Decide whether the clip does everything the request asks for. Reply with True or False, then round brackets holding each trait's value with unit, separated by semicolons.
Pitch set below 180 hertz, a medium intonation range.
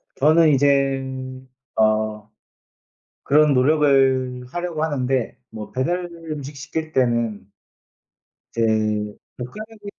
True (135 Hz; 3.4 semitones)